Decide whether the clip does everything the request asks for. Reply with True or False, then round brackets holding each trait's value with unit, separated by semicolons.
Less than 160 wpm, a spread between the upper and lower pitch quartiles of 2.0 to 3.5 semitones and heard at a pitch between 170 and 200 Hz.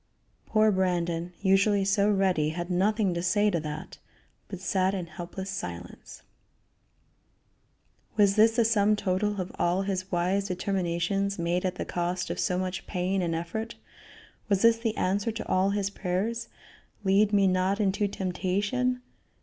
True (150 wpm; 2.4 semitones; 190 Hz)